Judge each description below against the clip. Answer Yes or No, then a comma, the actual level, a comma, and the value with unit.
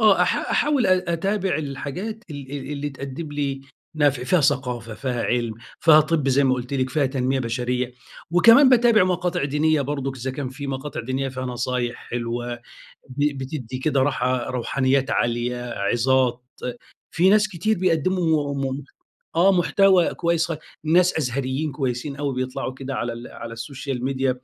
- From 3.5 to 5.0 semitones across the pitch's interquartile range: Yes, average, 4.1 semitones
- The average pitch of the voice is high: No, low, 135 Hz